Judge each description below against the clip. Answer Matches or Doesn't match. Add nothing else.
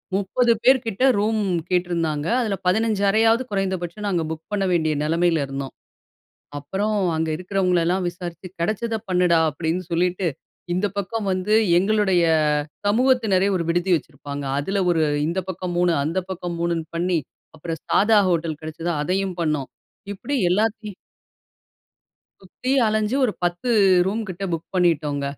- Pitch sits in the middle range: Matches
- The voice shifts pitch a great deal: Doesn't match